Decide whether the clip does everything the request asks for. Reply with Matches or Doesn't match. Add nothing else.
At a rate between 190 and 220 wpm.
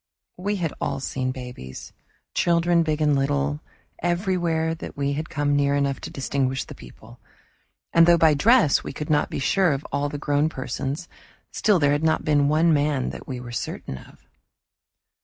Doesn't match